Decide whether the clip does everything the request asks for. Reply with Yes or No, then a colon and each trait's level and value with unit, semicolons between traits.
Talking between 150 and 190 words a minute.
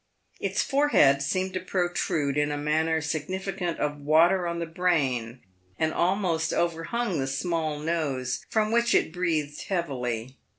No: average, 140 wpm